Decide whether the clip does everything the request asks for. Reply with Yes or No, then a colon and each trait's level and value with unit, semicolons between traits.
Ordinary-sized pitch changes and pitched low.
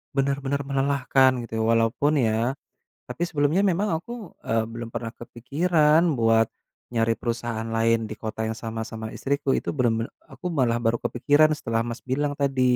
Yes: average, 3.8 semitones; low, 120 Hz